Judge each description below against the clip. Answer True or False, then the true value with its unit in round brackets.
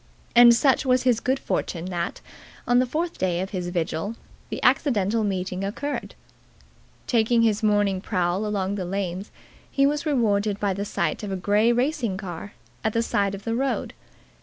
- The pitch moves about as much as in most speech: True (4.2 semitones)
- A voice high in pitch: True (210 Hz)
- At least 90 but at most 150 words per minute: False (175 wpm)